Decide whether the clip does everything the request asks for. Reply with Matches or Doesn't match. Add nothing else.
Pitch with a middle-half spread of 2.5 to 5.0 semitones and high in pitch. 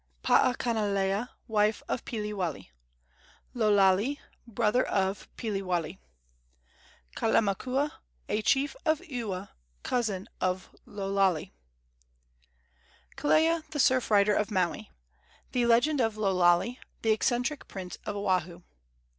Matches